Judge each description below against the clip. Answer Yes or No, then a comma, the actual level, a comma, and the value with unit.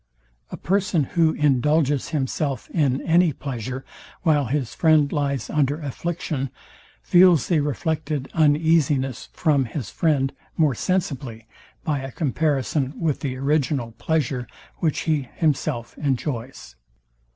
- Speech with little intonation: No, average, 3.1 semitones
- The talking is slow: Yes, slow, 120 wpm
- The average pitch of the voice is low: No, medium, 145 Hz